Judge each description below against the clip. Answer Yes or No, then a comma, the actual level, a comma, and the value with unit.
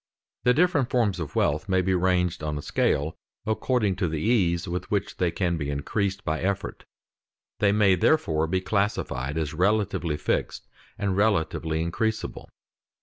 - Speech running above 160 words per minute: No, average, 155 wpm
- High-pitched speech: No, very low, 95 Hz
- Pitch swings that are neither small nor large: Yes, average, 4.4 semitones